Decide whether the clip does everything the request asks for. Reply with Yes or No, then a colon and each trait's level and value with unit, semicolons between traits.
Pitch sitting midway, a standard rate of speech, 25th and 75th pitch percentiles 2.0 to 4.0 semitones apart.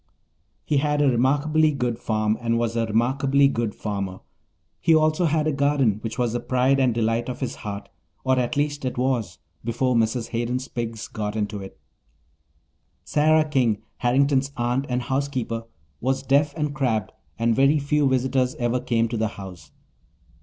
No: low, 125 Hz; average, 165 wpm; average, 3.4 semitones